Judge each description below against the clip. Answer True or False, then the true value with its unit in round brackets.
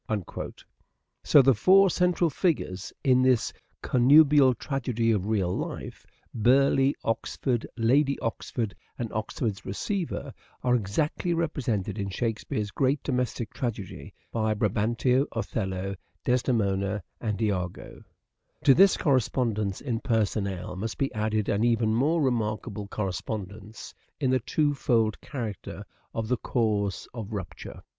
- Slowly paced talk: True (120 wpm)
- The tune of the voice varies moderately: True (4.1 semitones)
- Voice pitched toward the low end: True (115 Hz)